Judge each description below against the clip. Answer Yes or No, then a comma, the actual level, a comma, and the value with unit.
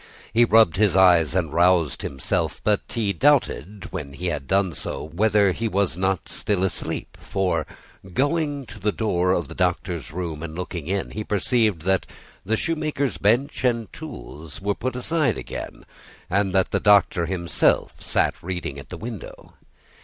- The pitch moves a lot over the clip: No, average, 4.3 semitones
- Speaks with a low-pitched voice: Yes, very low, 95 Hz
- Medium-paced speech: Yes, average, 165 wpm